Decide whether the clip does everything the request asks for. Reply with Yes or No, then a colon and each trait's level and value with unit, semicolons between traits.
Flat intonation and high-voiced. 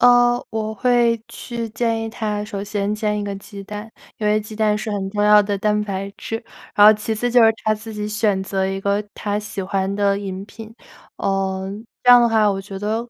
Yes: narrow, 1.9 semitones; high, 210 Hz